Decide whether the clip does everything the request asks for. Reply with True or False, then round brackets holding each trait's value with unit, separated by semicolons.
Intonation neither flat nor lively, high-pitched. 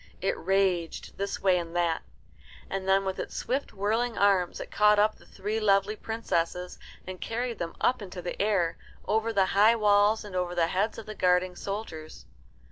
True (3.0 semitones; 195 Hz)